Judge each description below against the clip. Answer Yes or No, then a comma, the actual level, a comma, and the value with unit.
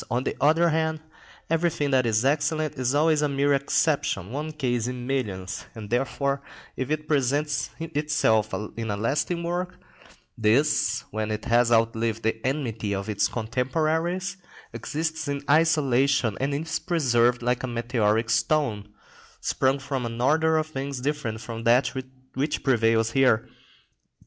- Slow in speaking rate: No, average, 145 wpm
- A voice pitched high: No, low, 135 Hz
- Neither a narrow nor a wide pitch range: Yes, average, 4.9 semitones